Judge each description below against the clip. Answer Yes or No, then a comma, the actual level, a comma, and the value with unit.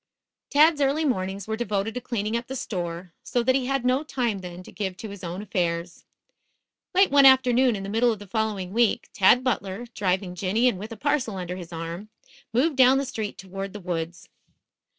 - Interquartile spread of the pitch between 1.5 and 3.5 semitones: No, average, 5.2 semitones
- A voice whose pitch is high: Yes, high, 215 Hz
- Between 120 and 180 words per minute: No, fast, 205 wpm